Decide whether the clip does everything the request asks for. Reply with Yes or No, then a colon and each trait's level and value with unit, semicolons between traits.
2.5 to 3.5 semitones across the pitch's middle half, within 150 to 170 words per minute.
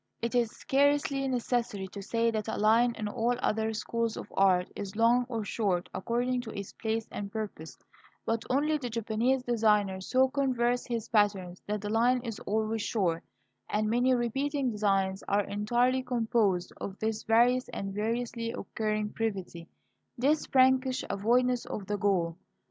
Yes: average, 3.1 semitones; average, 160 wpm